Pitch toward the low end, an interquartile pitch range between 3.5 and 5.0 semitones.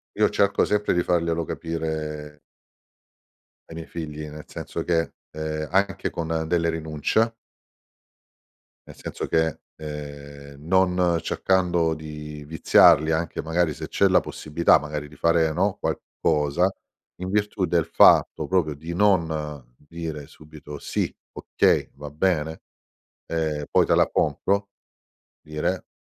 No: very low, 80 Hz; narrow, 2.4 semitones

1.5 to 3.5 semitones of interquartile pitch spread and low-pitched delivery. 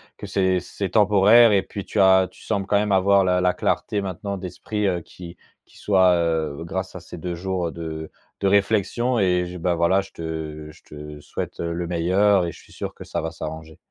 Yes: average, 2.8 semitones; very low, 90 Hz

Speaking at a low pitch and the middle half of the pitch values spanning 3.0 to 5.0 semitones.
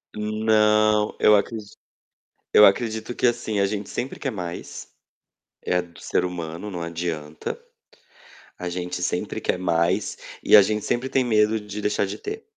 Yes: low, 105 Hz; average, 3.4 semitones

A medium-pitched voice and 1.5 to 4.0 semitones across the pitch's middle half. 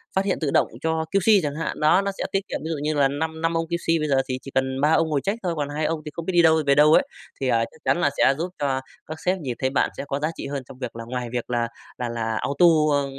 Yes: medium, 150 Hz; average, 3.6 semitones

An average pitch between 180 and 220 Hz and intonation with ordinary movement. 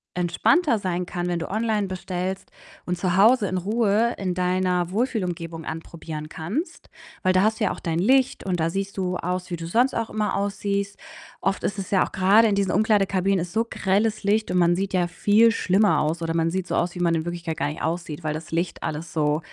Yes: medium, 185 Hz; average, 3.0 semitones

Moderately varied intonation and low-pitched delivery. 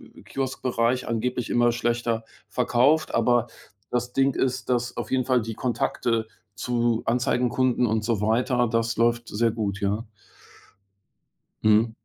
No: narrow, 1.6 semitones; low, 120 Hz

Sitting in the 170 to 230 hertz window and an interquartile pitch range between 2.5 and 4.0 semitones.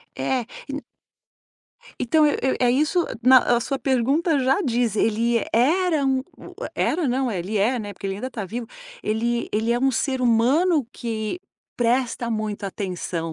No: high, 240 Hz; average, 3.6 semitones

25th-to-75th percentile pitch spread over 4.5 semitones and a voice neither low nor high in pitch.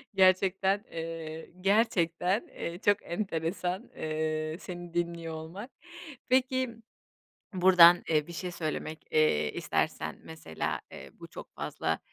No: average, 3.0 semitones; medium, 170 Hz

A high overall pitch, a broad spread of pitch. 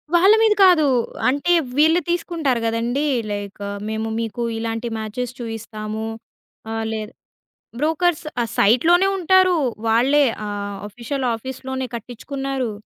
Yes: very high, 250 Hz; wide, 5.7 semitones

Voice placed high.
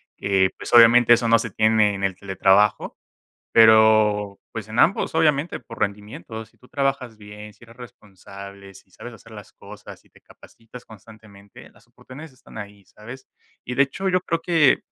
No: low, 110 Hz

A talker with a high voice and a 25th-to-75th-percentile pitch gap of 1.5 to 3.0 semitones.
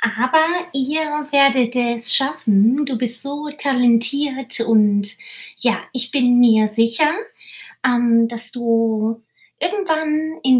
No: high, 245 Hz; average, 3.6 semitones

